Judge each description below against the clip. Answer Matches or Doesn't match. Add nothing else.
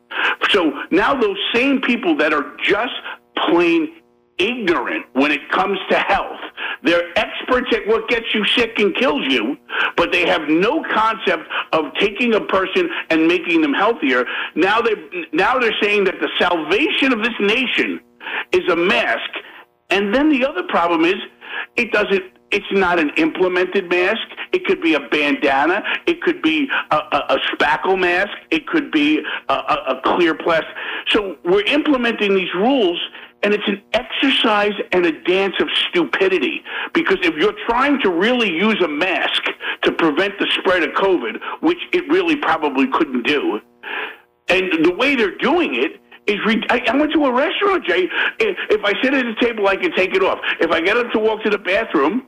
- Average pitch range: Doesn't match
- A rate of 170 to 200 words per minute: Matches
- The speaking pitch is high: Matches